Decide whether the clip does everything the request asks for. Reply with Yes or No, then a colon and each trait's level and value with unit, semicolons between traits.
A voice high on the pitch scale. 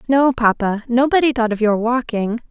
Yes: high, 240 Hz